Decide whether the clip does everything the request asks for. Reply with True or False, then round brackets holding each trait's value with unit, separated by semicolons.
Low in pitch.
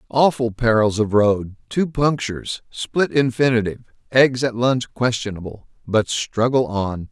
True (120 Hz)